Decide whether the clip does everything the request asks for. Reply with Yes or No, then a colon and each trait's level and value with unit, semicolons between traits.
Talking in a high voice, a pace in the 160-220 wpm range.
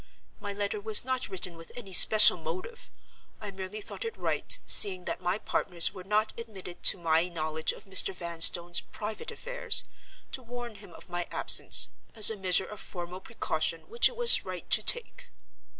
Yes: high, 195 Hz; average, 170 wpm